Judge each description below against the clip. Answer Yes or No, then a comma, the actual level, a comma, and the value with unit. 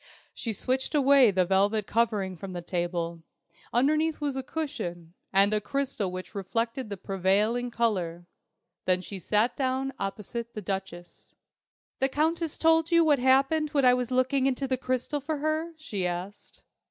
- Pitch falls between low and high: No, high, 235 Hz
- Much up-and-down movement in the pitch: Yes, wide, 6.2 semitones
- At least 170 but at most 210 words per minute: No, average, 160 wpm